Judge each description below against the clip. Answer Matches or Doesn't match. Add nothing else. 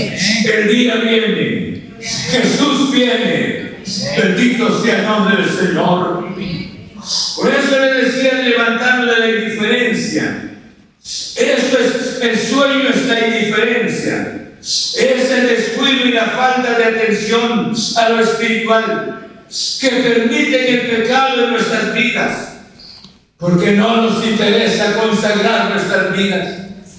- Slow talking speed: Matches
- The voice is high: Matches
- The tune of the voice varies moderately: Doesn't match